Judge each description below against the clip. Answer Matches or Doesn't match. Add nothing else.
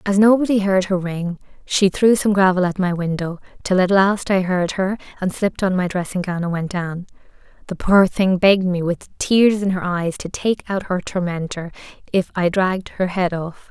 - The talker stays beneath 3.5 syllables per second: Doesn't match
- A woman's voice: Matches